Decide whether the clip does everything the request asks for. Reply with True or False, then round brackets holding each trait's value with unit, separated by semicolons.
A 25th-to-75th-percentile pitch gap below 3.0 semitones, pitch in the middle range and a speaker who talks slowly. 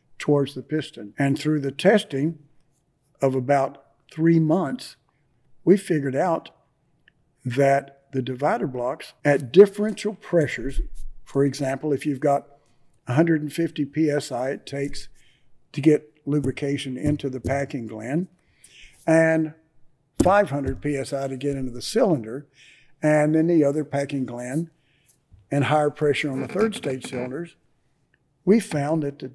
True (2.4 semitones; 145 Hz; 130 wpm)